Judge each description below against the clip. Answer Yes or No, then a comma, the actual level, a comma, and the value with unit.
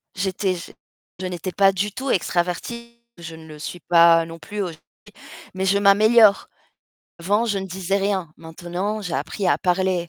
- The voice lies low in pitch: No, medium, 185 Hz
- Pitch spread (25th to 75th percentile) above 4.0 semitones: No, average, 2.8 semitones